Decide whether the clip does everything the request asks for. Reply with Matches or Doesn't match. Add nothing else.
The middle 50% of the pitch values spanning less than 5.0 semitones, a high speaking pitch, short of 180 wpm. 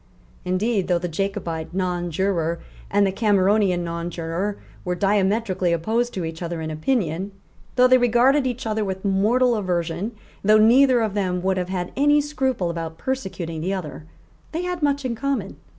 Doesn't match